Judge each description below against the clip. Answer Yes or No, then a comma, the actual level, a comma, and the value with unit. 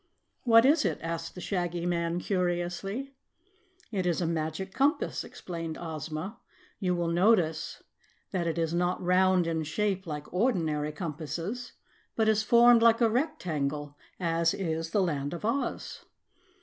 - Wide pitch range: No, average, 4.2 semitones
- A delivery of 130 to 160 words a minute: Yes, average, 145 wpm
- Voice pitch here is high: No, medium, 175 Hz